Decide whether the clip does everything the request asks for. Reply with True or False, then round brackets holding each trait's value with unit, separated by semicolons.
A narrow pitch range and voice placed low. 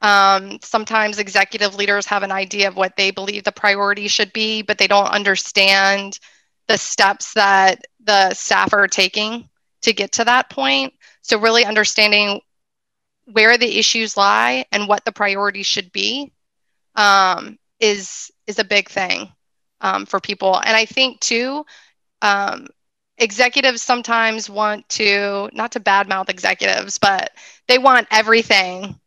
False (2.3 semitones; 205 Hz)